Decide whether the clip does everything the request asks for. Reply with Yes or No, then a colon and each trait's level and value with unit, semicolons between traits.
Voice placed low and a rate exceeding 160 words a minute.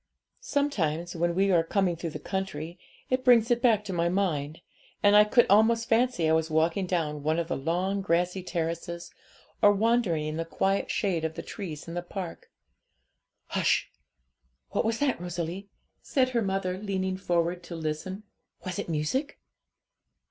No: medium, 180 Hz; average, 170 wpm